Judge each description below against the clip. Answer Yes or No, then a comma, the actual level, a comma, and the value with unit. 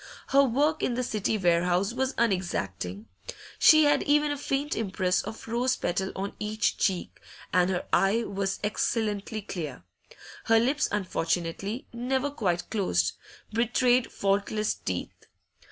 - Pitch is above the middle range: Yes, high, 210 Hz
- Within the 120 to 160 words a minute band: Yes, slow, 135 wpm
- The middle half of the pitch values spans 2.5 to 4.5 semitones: No, average, 5.3 semitones